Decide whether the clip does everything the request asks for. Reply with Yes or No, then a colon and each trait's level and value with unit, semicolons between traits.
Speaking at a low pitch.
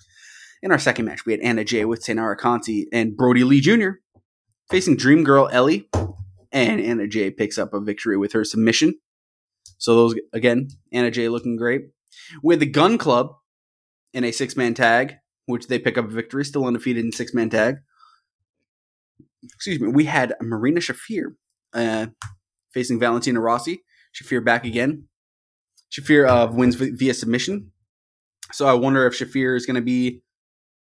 Yes: low, 120 Hz